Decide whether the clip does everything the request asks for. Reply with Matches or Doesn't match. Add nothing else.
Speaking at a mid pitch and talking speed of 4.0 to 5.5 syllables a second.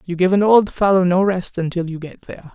Doesn't match